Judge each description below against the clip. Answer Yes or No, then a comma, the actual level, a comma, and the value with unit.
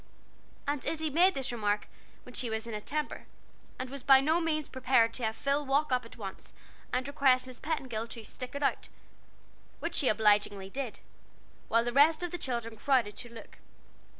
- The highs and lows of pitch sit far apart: No, average, 3.9 semitones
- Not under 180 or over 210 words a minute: Yes, average, 190 wpm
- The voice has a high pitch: Yes, very high, 255 Hz